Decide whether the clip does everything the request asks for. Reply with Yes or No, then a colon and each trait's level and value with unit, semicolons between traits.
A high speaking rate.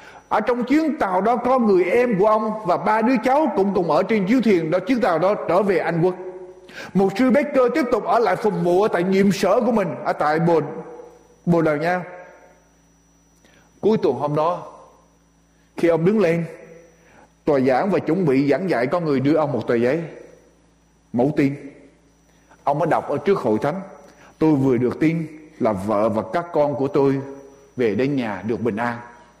No: average, 200 wpm